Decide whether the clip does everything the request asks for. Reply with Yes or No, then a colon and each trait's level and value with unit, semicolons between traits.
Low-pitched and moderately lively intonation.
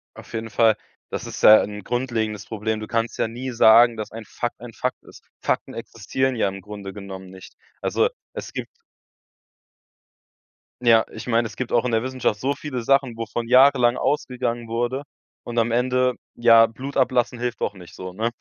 No: low, 115 Hz; narrow, 2.3 semitones